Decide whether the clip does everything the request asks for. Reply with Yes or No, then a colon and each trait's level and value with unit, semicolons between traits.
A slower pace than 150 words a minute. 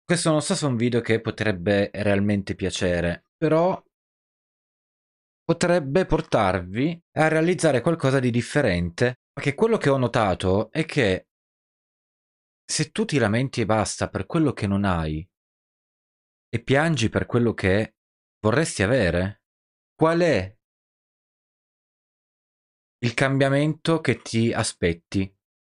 Yes: average, 120 wpm